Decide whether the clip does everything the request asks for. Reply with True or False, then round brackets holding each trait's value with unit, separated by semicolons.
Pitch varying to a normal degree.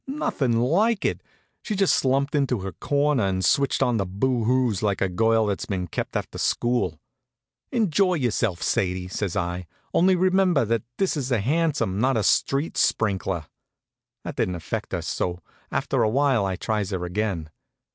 False (6.9 semitones)